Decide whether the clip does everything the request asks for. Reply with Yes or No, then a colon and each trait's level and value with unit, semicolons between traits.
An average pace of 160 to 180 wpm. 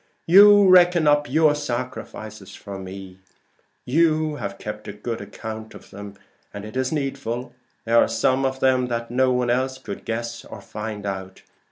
Yes: average, 170 wpm